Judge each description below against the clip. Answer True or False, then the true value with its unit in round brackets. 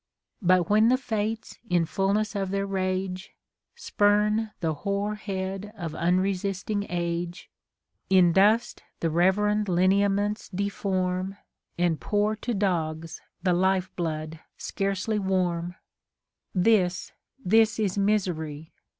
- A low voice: False (190 Hz)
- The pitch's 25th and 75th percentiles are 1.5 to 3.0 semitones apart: True (2.7 semitones)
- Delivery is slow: True (110 wpm)